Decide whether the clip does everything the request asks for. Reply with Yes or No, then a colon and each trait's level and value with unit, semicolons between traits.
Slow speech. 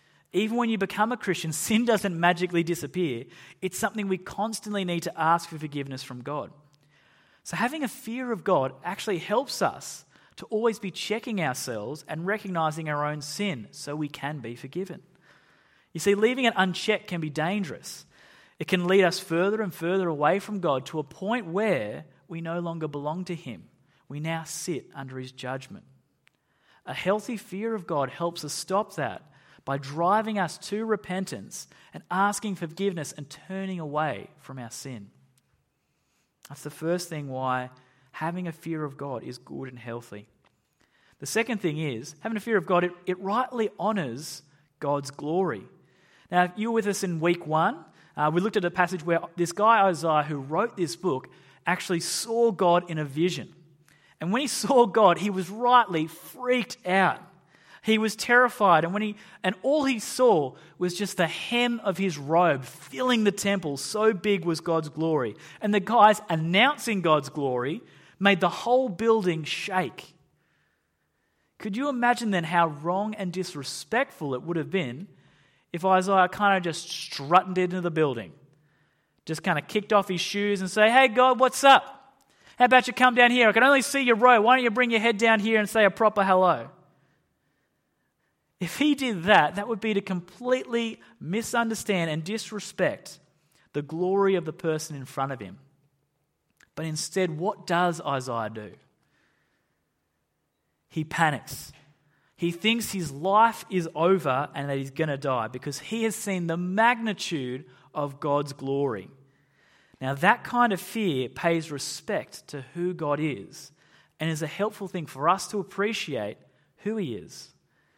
No: average, 170 wpm